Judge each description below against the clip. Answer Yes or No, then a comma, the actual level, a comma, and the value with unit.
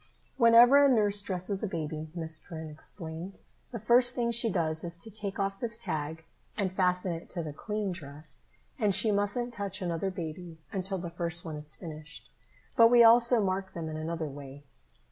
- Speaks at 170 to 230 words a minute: Yes, average, 185 wpm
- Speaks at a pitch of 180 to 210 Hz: Yes, medium, 185 Hz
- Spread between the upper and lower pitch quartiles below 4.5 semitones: No, average, 4.8 semitones